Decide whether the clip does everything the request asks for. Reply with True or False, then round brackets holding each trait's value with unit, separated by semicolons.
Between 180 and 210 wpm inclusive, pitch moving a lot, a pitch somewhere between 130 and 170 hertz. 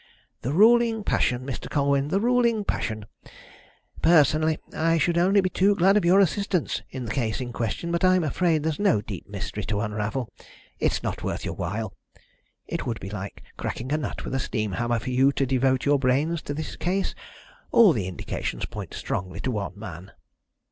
True (190 wpm; 7.7 semitones; 140 Hz)